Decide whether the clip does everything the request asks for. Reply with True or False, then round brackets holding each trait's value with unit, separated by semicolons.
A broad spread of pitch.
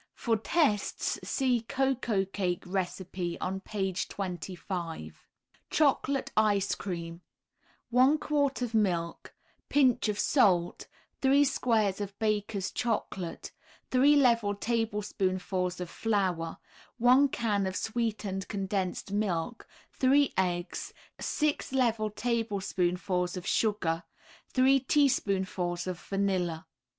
False (4.7 semitones)